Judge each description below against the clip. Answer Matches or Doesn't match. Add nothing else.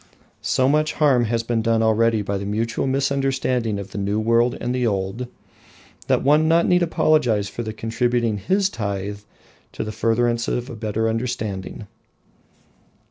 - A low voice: Matches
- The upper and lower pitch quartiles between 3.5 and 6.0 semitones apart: Doesn't match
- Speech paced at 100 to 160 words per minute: Matches